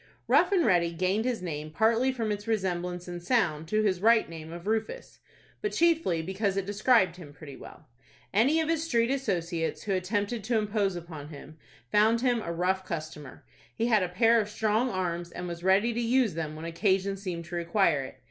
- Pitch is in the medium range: No, high, 195 Hz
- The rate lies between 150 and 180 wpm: No, average, 200 wpm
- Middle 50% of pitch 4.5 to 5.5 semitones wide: Yes, average, 4.9 semitones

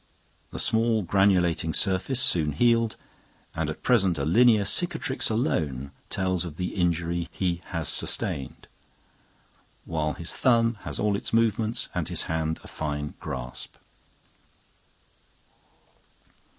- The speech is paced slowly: Yes, slow, 120 wpm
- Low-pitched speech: Yes, very low, 90 Hz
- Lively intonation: Yes, wide, 5.8 semitones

